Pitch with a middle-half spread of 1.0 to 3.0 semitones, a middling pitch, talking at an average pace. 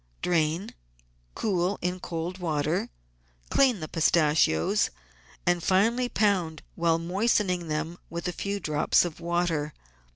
No: narrow, 2.6 semitones; medium, 175 Hz; slow, 120 wpm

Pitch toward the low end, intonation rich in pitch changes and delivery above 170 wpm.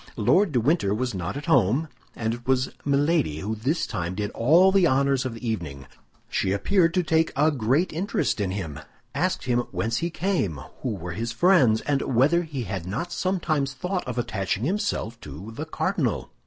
Yes: low, 130 Hz; wide, 7.5 semitones; average, 190 wpm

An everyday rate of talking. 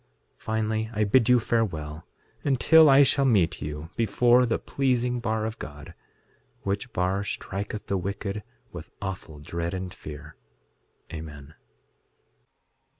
No: slow, 130 wpm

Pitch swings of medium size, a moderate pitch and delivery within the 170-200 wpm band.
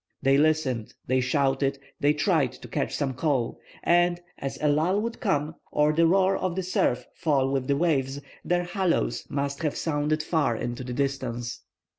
Yes: average, 3.8 semitones; medium, 145 Hz; average, 175 wpm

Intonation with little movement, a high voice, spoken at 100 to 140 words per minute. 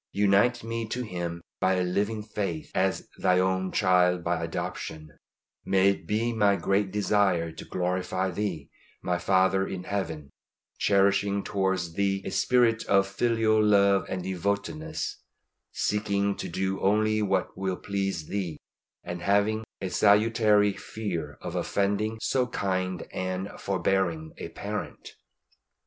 No: narrow, 2.2 semitones; very low, 95 Hz; slow, 135 wpm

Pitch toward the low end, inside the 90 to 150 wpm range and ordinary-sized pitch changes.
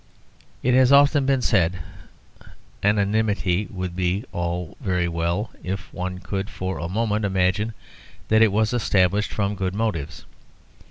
Yes: low, 100 Hz; average, 140 wpm; average, 3.3 semitones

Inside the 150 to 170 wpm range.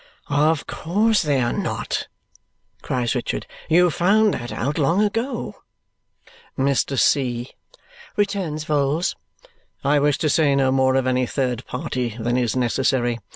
No: slow, 135 wpm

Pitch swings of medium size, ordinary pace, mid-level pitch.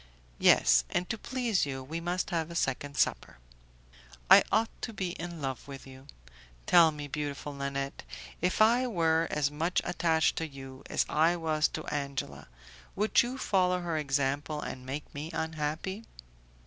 Yes: average, 4.0 semitones; average, 160 wpm; medium, 155 Hz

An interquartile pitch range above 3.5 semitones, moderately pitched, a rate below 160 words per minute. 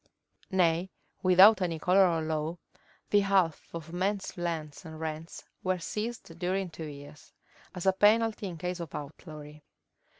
No: average, 3.2 semitones; medium, 175 Hz; average, 145 wpm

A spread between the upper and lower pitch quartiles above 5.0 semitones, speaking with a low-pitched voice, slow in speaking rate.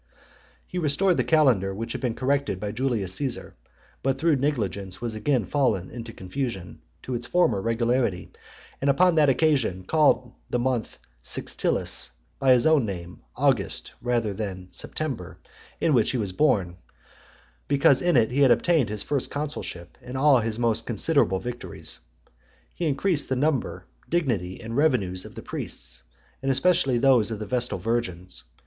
No: wide, 5.6 semitones; low, 120 Hz; average, 160 wpm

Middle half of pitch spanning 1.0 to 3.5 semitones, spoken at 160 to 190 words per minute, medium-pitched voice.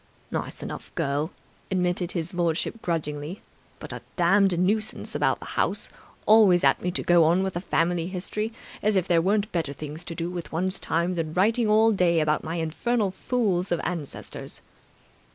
Yes: average, 2.9 semitones; average, 175 wpm; medium, 175 Hz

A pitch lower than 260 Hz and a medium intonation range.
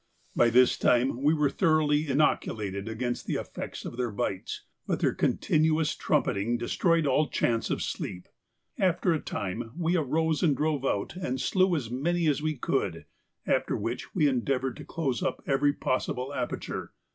Yes: medium, 140 Hz; average, 4.5 semitones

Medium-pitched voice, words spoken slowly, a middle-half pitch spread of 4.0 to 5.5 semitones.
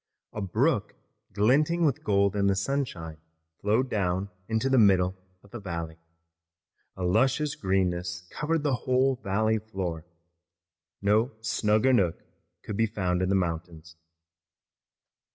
No: low, 100 Hz; slow, 125 wpm; average, 5.1 semitones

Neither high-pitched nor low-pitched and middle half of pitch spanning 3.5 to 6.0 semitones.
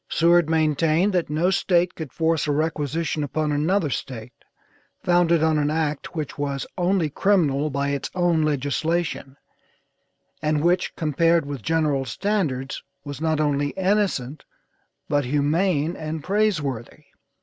No: medium, 155 Hz; average, 3.1 semitones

